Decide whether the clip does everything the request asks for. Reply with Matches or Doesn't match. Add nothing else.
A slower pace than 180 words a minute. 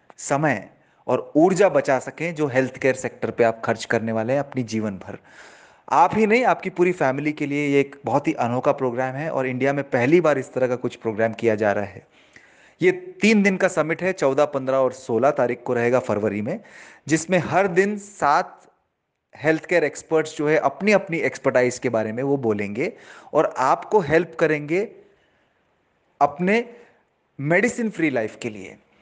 Doesn't match